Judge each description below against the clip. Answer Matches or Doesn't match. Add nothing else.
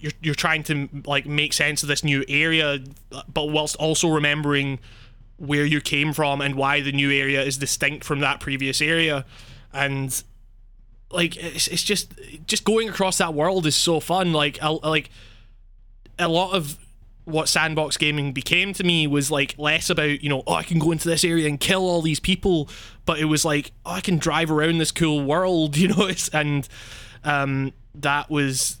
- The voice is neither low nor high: Matches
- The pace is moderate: Matches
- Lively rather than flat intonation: Doesn't match